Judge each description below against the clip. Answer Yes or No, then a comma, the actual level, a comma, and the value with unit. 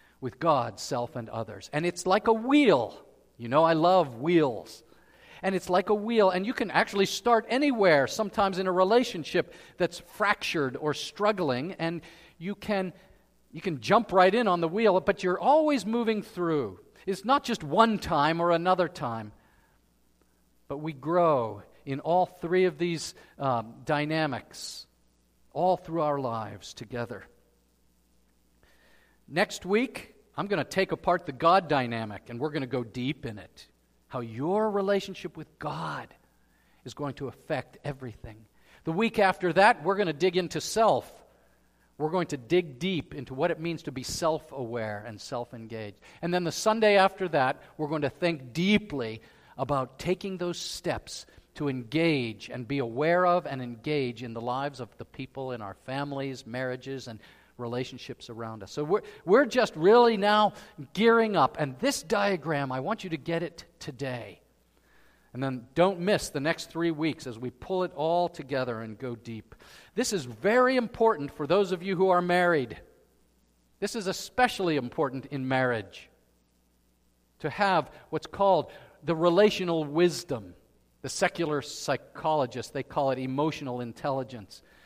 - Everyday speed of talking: Yes, average, 165 wpm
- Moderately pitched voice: Yes, medium, 155 Hz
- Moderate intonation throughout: No, wide, 7.1 semitones